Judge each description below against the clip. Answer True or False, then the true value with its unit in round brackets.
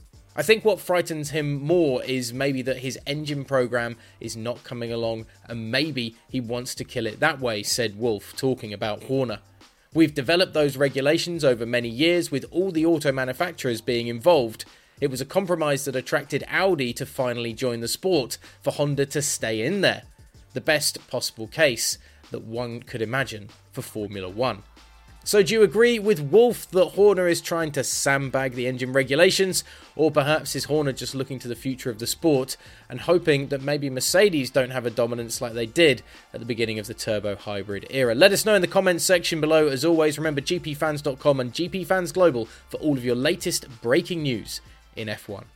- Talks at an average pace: True (190 wpm)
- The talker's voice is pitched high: False (135 Hz)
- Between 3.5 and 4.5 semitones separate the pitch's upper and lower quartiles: False (5.0 semitones)